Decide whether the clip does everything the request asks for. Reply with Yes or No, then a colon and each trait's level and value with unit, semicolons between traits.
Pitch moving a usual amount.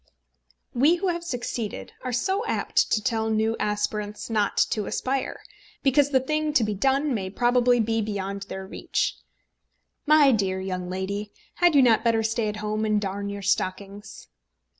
Yes: average, 4.4 semitones